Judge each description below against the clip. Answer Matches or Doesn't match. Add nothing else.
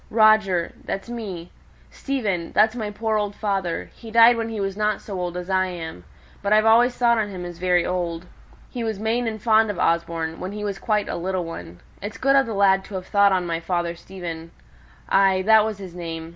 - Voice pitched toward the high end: Matches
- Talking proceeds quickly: Matches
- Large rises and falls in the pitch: Doesn't match